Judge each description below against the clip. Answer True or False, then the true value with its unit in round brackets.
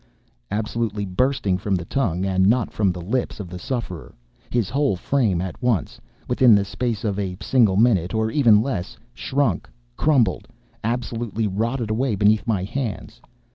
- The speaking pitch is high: False (105 Hz)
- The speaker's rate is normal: True (145 wpm)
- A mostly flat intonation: False (4.4 semitones)